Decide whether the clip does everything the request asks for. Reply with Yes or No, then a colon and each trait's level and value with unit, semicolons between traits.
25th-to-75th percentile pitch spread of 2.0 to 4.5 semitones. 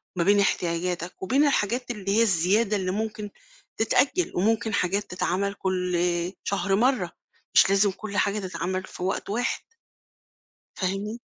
Yes: average, 2.8 semitones